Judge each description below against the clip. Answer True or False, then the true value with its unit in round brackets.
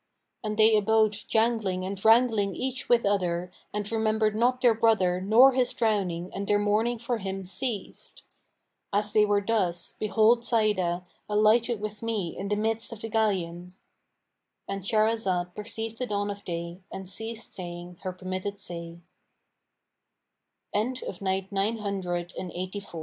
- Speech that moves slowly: True (130 wpm)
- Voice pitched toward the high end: True (210 Hz)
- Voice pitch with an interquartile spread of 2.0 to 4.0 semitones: True (3.1 semitones)